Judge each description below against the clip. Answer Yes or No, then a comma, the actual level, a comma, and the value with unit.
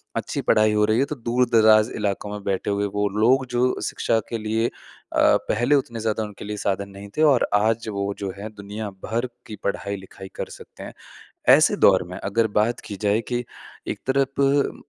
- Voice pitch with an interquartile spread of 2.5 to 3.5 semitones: Yes, average, 3.0 semitones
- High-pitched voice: No, low, 110 Hz